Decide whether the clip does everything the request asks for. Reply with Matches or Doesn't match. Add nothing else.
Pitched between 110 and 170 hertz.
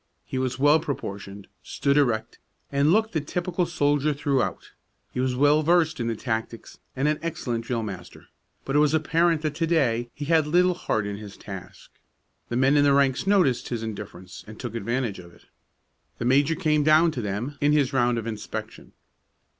Matches